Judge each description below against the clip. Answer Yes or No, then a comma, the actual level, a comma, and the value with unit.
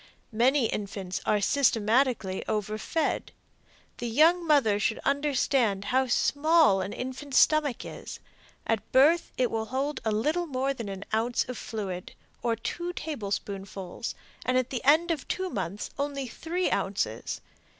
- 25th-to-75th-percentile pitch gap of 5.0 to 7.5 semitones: Yes, wide, 5.6 semitones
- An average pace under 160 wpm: Yes, average, 140 wpm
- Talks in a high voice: Yes, very high, 250 Hz